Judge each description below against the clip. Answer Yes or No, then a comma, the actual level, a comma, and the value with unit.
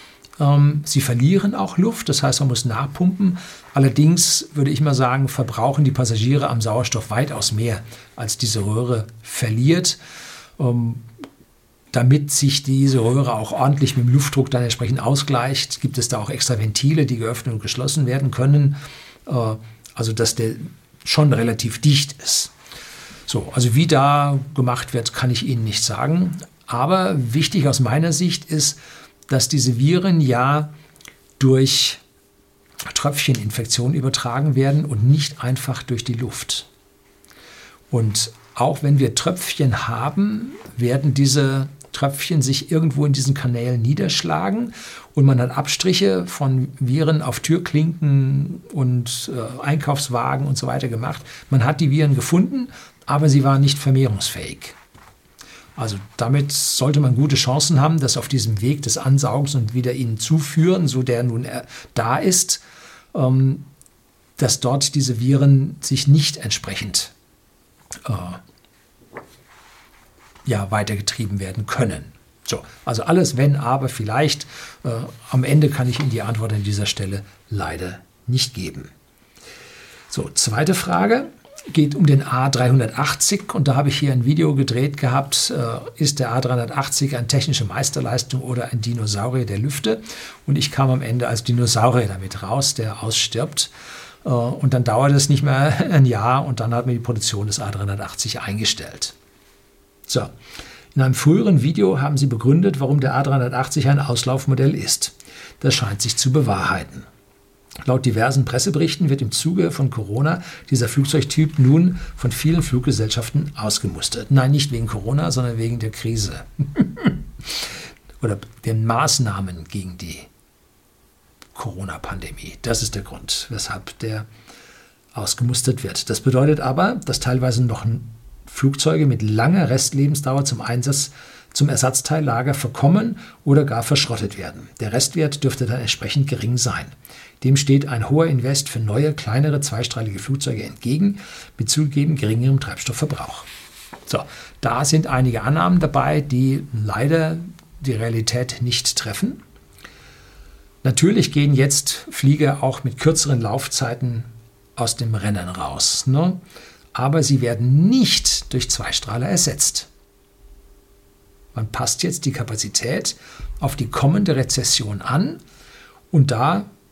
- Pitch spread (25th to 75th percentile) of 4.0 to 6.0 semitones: No, average, 3.5 semitones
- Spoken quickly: No, average, 135 wpm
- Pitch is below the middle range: Yes, low, 130 Hz